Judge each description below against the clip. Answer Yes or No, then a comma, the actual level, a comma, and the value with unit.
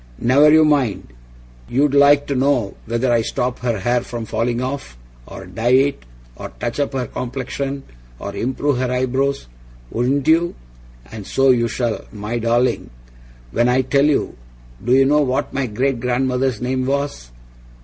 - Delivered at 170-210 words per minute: No, average, 160 wpm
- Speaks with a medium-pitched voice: No, low, 130 Hz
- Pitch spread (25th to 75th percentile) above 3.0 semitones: No, narrow, 2.6 semitones